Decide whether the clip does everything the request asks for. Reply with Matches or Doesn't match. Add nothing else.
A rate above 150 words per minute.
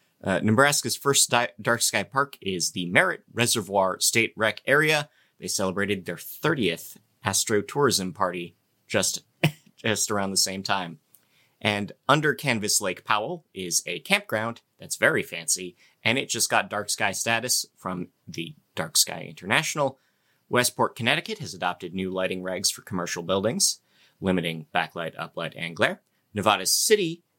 Doesn't match